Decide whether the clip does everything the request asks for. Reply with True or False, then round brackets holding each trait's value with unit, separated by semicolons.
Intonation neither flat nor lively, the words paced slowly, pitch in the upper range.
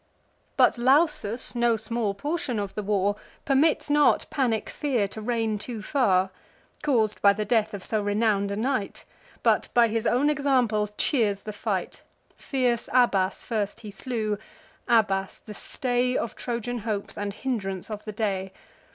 False (3.4 semitones; 155 wpm; 220 Hz)